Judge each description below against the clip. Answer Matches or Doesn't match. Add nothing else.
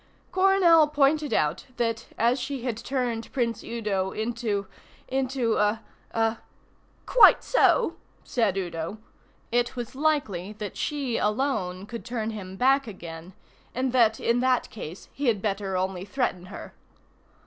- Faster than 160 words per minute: Doesn't match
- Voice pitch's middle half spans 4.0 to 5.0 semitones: Matches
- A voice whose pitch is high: Matches